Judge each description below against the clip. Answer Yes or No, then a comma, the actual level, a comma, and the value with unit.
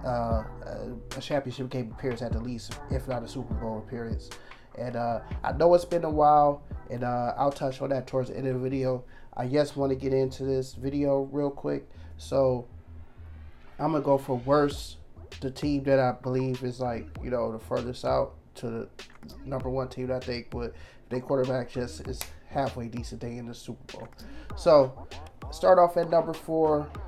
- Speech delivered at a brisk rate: No, average, 195 wpm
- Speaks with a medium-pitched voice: No, low, 130 Hz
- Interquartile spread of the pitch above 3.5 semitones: No, narrow, 2.5 semitones